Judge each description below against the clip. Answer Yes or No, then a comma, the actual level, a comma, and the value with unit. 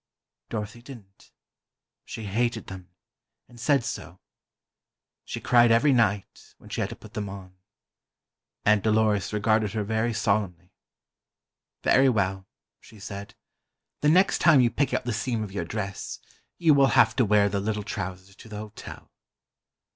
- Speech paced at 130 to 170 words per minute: Yes, average, 155 wpm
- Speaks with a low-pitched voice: Yes, low, 105 Hz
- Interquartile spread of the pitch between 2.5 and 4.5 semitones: Yes, average, 3.1 semitones